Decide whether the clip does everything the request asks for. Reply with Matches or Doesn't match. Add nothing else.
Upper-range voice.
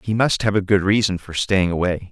Doesn't match